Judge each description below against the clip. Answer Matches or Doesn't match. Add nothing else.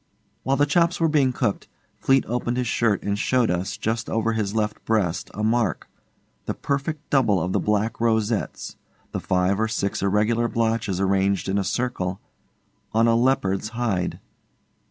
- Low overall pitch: Matches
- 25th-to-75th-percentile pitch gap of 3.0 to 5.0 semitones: Matches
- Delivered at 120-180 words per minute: Matches